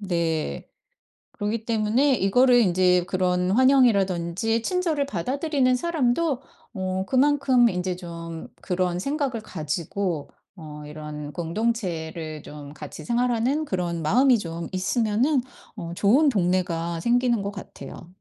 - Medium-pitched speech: No, high, 195 Hz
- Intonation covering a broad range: Yes, wide, 6.5 semitones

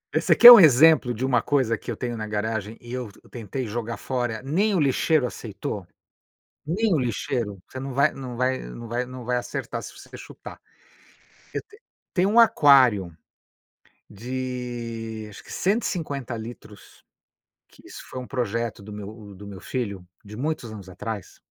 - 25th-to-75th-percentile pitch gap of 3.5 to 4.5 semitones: Yes, average, 3.8 semitones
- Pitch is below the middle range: Yes, low, 120 Hz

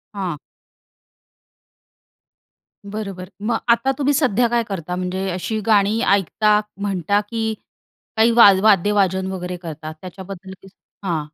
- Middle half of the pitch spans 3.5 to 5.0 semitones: No, average, 3.1 semitones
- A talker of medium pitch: No, high, 195 Hz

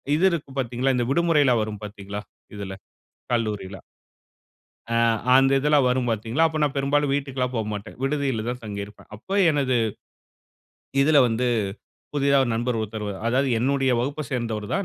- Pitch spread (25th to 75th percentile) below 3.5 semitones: No, average, 4.3 semitones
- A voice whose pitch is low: Yes, low, 125 Hz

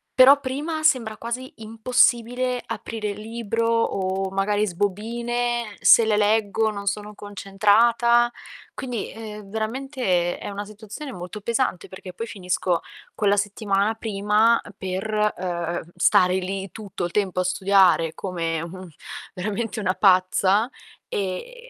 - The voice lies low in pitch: No, high, 210 Hz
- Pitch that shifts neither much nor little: Yes, average, 3.3 semitones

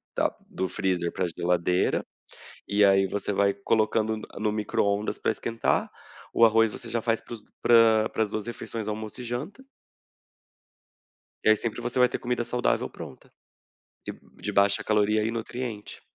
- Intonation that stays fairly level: Yes, narrow, 2.2 semitones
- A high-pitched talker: No, low, 110 Hz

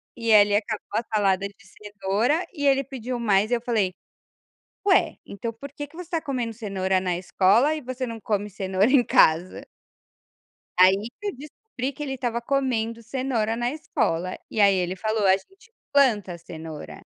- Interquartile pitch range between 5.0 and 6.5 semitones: Yes, average, 5.3 semitones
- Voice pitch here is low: No, high, 225 Hz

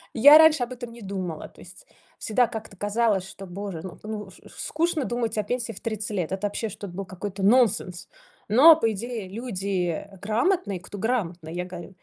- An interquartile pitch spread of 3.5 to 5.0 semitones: Yes, average, 4.1 semitones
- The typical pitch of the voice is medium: No, high, 205 Hz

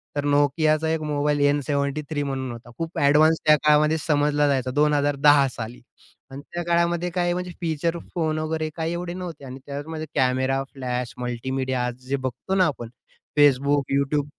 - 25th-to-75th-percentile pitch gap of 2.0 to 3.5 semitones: Yes, average, 2.8 semitones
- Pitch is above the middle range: No, medium, 145 Hz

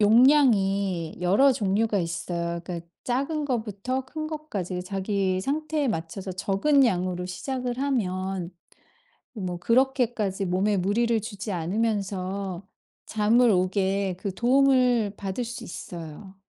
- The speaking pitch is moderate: No, high, 200 Hz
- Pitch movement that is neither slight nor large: Yes, average, 4.9 semitones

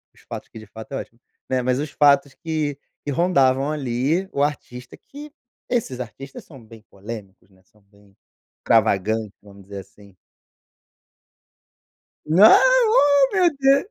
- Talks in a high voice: No, low, 130 Hz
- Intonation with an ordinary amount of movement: No, wide, 7.3 semitones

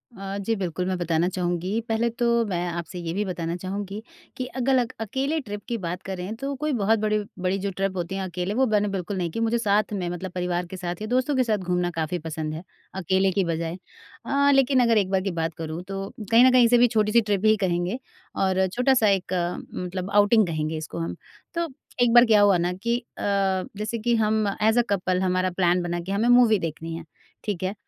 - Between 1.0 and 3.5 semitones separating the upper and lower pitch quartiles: No, average, 3.9 semitones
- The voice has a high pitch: Yes, high, 195 Hz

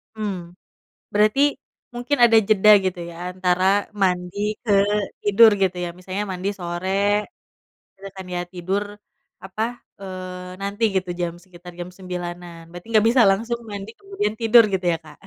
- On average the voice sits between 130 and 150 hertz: No, high, 190 Hz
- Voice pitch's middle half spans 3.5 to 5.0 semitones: No, average, 2.9 semitones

